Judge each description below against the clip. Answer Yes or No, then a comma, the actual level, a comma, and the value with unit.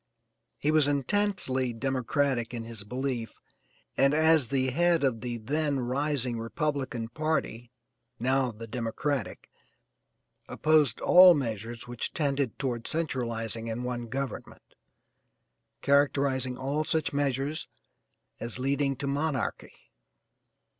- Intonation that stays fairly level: No, average, 3.4 semitones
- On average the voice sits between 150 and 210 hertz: No, low, 135 Hz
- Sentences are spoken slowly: Yes, slow, 110 wpm